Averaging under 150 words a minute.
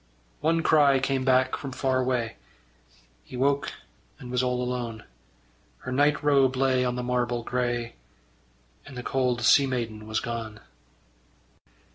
Yes: average, 140 wpm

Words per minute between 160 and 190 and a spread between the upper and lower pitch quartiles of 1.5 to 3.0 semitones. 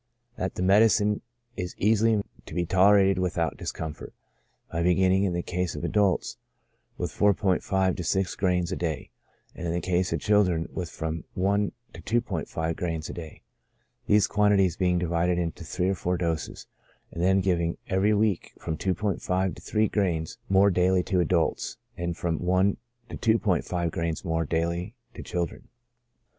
Yes: average, 165 wpm; narrow, 2.5 semitones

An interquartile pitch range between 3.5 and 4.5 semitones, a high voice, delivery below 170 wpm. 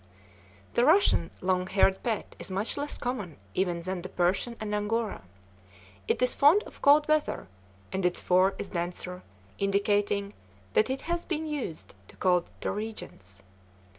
No: wide, 5.4 semitones; high, 200 Hz; average, 150 wpm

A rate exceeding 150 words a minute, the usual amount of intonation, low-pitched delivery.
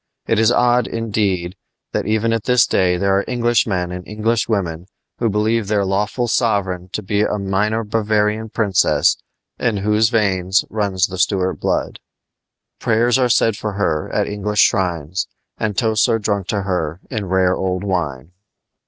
Yes: average, 160 wpm; average, 3.0 semitones; low, 105 Hz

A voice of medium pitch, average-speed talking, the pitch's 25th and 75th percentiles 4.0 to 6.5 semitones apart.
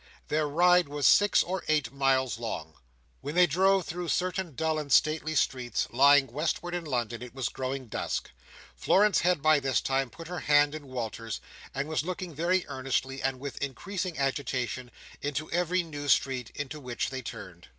Yes: medium, 145 Hz; average, 175 wpm; average, 4.3 semitones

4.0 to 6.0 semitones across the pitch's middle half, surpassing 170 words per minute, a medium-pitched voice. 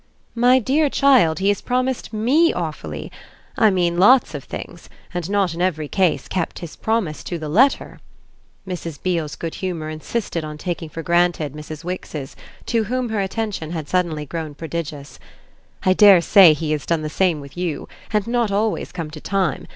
Yes: average, 5.2 semitones; average, 180 wpm; medium, 175 Hz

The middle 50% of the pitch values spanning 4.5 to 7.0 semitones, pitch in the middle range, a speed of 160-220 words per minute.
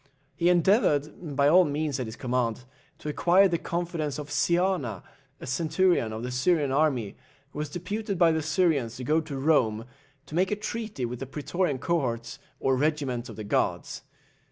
Yes: wide, 5.4 semitones; medium, 150 Hz; average, 180 wpm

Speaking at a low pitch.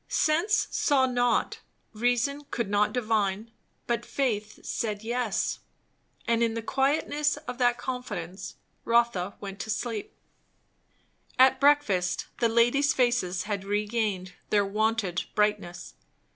No: high, 230 Hz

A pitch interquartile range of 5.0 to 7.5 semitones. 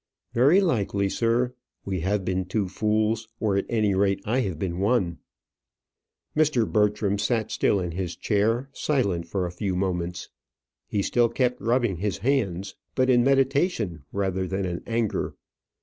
No: average, 4.2 semitones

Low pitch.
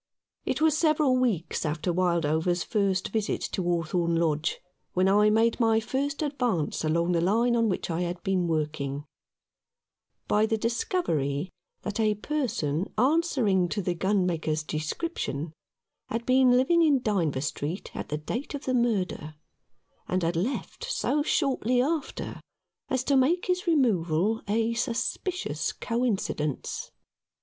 No: high, 210 Hz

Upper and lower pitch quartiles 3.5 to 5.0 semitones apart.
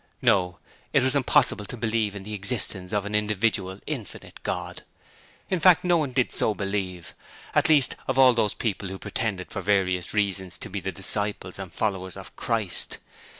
Yes: average, 3.8 semitones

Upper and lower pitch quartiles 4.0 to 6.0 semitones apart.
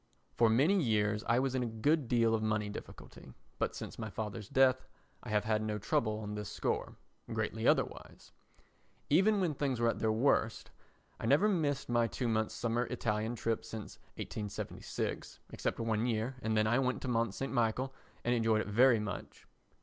No: average, 3.1 semitones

